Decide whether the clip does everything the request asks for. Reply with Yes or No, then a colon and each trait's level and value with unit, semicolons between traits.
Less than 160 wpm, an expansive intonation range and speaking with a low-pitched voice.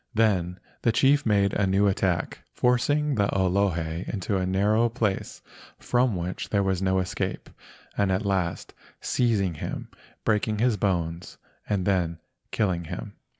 No: average, 145 wpm; average, 3.1 semitones; low, 100 Hz